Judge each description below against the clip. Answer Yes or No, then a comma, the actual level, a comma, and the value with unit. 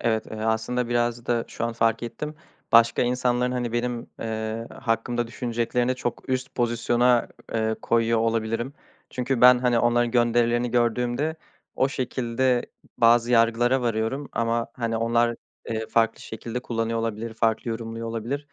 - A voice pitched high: No, low, 120 Hz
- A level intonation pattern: Yes, narrow, 1.3 semitones